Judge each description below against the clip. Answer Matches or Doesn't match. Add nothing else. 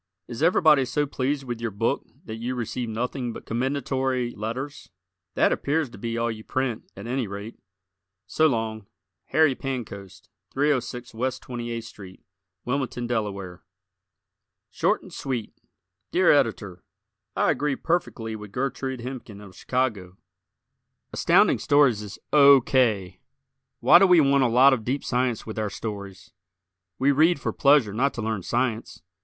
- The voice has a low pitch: Matches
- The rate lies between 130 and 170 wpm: Matches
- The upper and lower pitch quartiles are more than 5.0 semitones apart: Doesn't match